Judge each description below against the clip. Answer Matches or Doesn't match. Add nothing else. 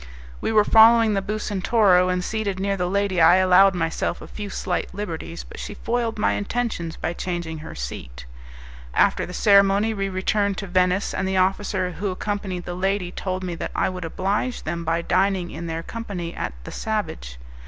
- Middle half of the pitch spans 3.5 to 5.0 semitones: Doesn't match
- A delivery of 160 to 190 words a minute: Matches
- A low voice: Doesn't match